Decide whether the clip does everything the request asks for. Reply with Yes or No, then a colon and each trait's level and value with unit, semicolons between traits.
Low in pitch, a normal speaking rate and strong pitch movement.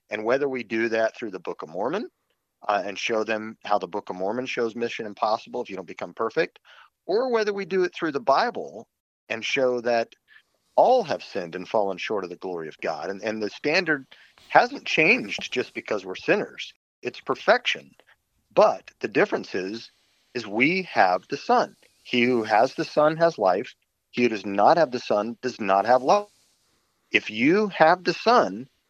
Yes: low, 125 Hz; average, 195 wpm; wide, 6.6 semitones